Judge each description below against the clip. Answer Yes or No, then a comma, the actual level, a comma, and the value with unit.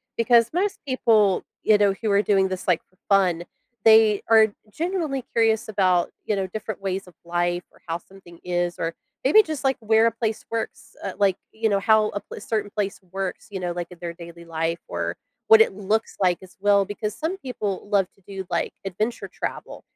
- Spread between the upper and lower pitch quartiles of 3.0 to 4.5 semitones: Yes, average, 3.5 semitones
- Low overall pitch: No, high, 200 Hz